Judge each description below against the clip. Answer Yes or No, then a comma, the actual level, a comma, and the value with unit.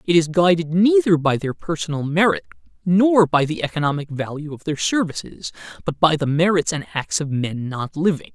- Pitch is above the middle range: No, medium, 160 Hz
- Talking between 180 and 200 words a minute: Yes, average, 185 wpm